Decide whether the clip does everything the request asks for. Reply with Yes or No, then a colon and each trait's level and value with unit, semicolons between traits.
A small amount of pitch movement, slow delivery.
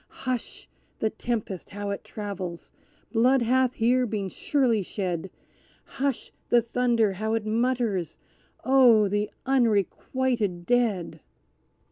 No: average, 3.6 semitones; slow, 110 wpm